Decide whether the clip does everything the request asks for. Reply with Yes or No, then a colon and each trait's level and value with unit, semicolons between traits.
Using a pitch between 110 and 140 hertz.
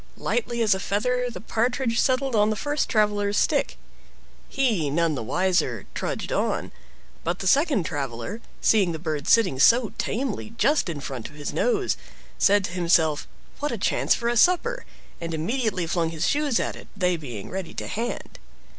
No: high, 205 Hz